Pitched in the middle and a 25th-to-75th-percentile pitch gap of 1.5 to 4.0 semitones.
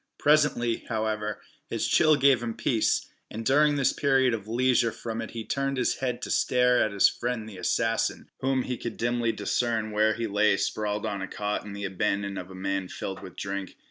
No: low, 115 Hz; average, 3.3 semitones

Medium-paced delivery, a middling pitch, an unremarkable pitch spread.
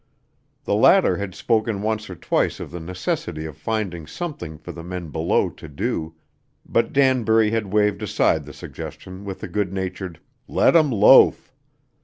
No: average, 165 wpm; low, 100 Hz; average, 4.2 semitones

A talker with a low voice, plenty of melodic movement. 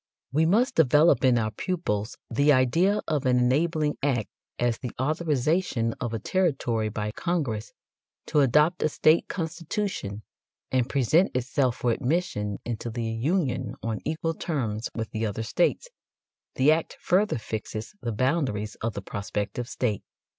Yes: low, 130 Hz; wide, 6.1 semitones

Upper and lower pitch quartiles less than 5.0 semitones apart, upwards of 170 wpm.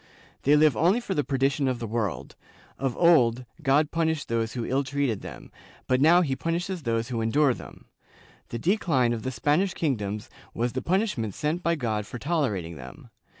No: wide, 5.6 semitones; average, 185 wpm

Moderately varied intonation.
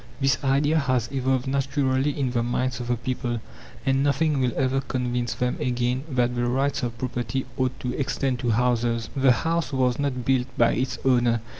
No: narrow, 1.8 semitones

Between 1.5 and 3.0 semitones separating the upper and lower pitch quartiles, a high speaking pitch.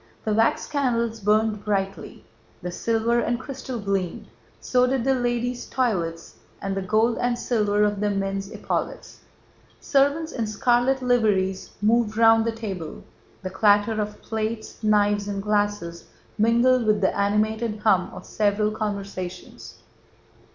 Yes: average, 2.7 semitones; high, 215 Hz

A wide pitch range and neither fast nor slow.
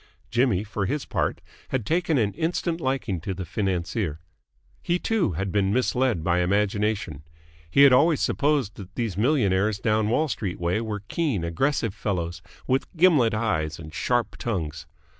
Yes: wide, 6.3 semitones; average, 160 wpm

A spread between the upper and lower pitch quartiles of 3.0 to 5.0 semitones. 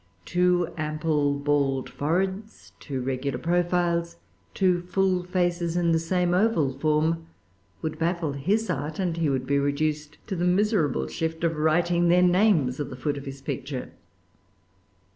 Yes: average, 3.6 semitones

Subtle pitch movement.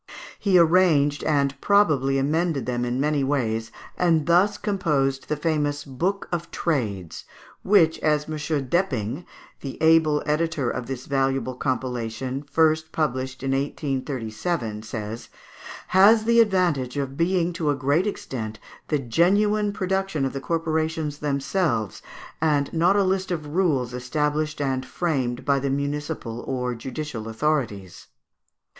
No: average, 4.3 semitones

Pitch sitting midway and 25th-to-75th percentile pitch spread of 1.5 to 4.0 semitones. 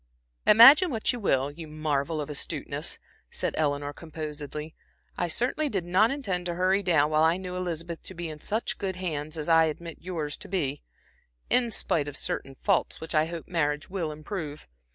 Yes: medium, 165 Hz; average, 3.7 semitones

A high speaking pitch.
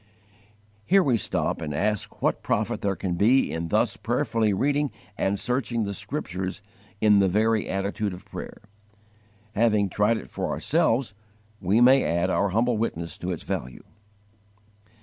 No: low, 105 Hz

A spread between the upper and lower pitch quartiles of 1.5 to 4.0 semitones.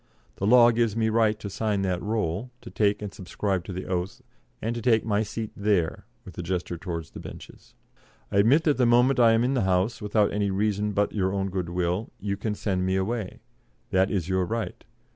Yes: average, 3.2 semitones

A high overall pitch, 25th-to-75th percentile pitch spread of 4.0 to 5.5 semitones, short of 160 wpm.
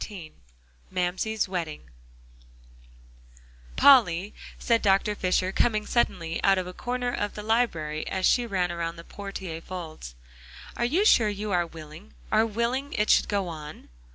Yes: high, 195 Hz; average, 4.6 semitones; average, 150 wpm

